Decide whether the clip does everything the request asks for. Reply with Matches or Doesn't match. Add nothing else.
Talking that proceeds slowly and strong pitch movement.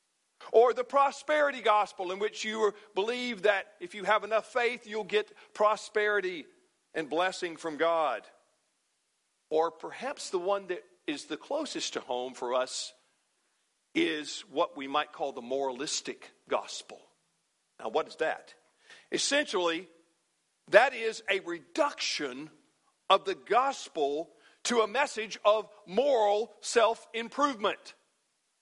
Matches